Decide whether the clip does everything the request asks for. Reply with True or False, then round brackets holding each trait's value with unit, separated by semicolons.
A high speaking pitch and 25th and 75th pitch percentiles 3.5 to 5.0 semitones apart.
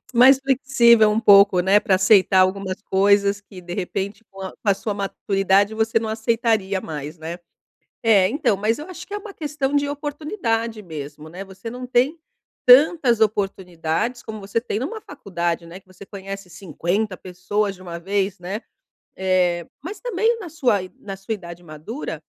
True (200 Hz; 4.3 semitones)